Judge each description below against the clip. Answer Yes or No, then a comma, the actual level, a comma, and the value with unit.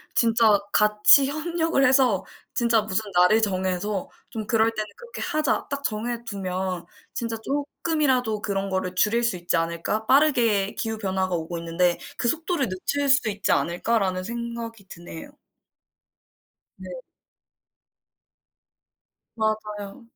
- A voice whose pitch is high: Yes, high, 215 Hz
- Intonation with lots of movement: No, average, 4.3 semitones